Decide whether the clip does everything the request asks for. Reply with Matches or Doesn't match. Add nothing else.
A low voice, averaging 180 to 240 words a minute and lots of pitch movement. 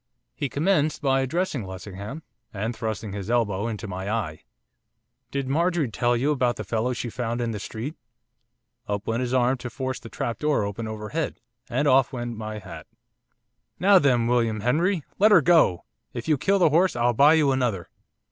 Doesn't match